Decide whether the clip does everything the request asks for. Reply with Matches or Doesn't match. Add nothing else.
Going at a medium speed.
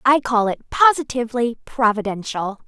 Doesn't match